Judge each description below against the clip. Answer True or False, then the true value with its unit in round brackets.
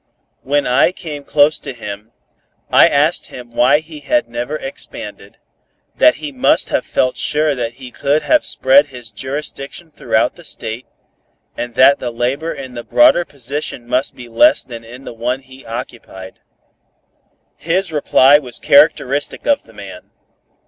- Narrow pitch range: False (3.8 semitones)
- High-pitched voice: False (135 Hz)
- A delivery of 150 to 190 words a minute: True (155 wpm)